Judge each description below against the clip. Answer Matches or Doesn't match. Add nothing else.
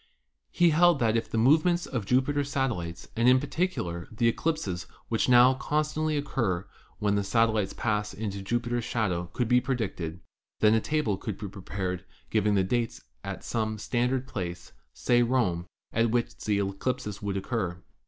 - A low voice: Matches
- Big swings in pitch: Doesn't match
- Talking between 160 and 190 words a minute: Matches